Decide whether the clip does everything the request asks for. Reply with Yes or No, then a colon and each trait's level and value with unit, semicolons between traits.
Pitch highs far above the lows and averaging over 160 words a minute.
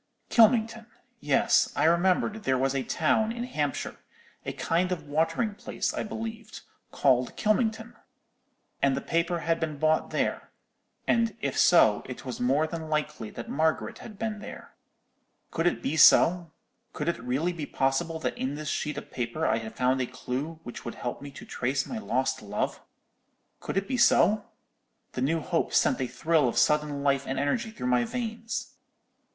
Yes: wide, 7.4 semitones; average, 170 wpm